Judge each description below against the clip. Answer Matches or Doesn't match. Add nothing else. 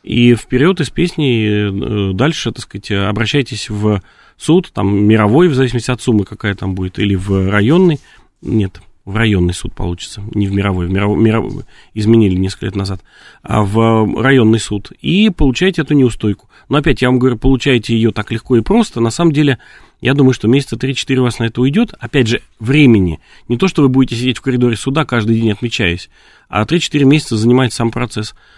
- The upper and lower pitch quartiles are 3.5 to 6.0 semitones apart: Matches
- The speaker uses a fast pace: Matches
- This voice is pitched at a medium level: Doesn't match